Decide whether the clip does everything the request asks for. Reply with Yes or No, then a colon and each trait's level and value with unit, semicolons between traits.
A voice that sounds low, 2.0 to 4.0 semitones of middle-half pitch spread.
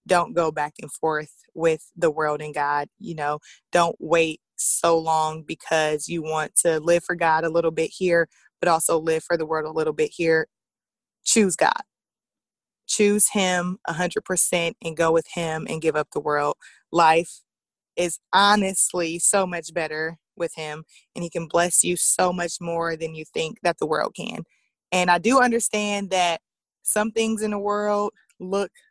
No: medium, 170 Hz; average, 2.8 semitones